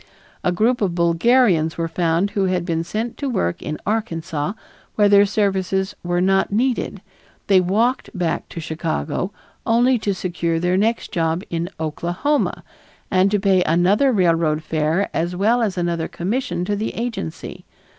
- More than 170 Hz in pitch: Yes, medium, 185 Hz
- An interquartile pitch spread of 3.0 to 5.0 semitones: Yes, average, 3.9 semitones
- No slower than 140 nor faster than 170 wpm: Yes, average, 155 wpm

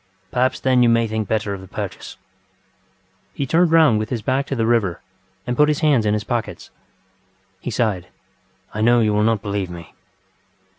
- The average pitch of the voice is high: No, low, 115 Hz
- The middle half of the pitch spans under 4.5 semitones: Yes, average, 3.5 semitones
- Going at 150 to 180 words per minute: No, average, 190 wpm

